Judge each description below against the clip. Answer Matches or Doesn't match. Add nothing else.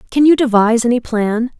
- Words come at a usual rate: Matches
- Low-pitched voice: Doesn't match